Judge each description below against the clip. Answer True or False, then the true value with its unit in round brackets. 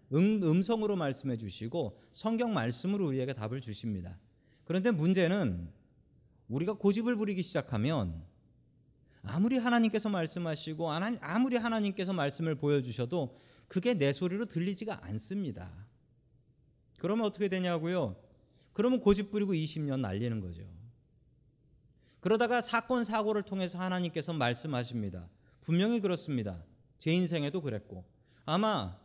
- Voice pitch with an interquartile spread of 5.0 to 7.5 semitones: False (8.7 semitones)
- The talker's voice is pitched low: False (160 Hz)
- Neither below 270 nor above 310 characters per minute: False (320 characters per minute)